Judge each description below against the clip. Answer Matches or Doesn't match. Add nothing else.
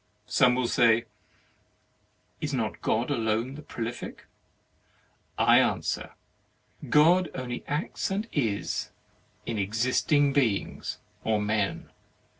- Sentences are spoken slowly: Matches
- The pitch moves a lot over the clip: Doesn't match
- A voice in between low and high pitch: Doesn't match